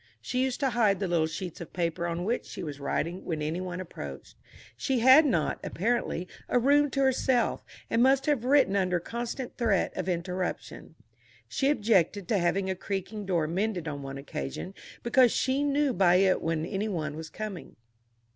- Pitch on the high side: Yes, high, 195 Hz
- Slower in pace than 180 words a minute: No, average, 185 wpm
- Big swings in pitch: Yes, wide, 6.2 semitones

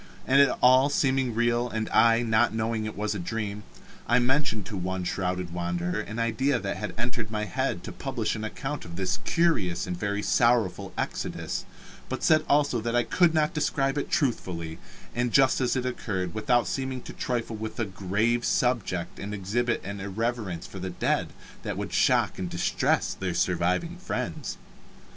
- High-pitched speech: No, low, 115 Hz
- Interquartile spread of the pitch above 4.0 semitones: Yes, average, 4.4 semitones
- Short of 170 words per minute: No, average, 180 wpm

